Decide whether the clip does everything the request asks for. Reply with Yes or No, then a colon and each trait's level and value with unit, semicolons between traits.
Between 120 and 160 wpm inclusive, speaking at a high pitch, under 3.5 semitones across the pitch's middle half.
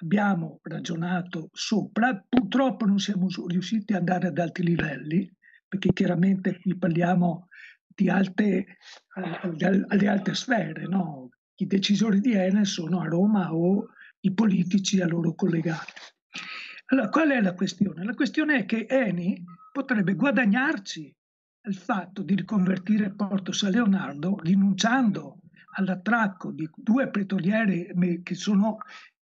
Yes: average, 130 wpm; high, 195 Hz; average, 2.8 semitones